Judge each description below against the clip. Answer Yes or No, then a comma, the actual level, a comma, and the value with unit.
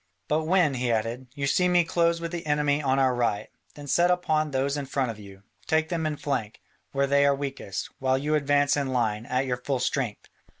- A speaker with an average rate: No, fast, 220 wpm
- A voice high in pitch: No, medium, 140 Hz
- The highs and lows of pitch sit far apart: No, average, 3.3 semitones